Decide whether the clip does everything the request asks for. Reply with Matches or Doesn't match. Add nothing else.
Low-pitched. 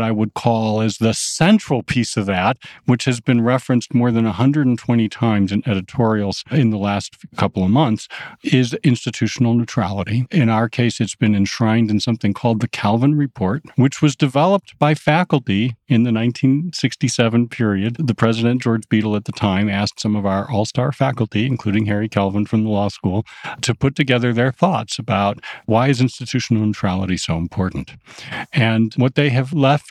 Matches